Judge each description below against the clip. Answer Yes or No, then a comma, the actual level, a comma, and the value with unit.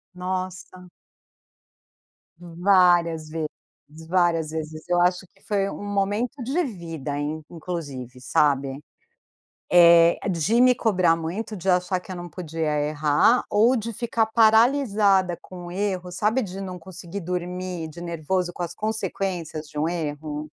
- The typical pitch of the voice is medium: Yes, medium, 180 Hz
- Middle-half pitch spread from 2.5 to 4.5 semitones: Yes, average, 3.5 semitones